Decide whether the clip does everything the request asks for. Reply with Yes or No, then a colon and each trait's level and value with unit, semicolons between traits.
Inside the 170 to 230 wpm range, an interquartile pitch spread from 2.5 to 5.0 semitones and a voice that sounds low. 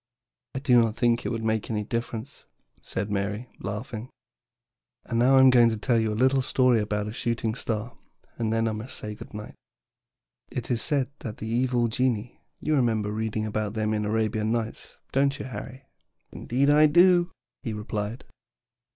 Yes: average, 185 wpm; average, 3.0 semitones; low, 115 Hz